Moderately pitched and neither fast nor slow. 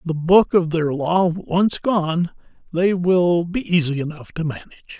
Yes: medium, 170 Hz; average, 170 wpm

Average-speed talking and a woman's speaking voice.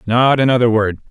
No: average, 160 wpm; male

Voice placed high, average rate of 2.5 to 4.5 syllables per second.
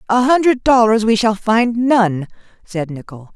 Yes: high, 220 Hz; 4.3 syllables/s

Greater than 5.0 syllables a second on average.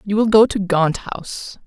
No: 4.6 syllables/s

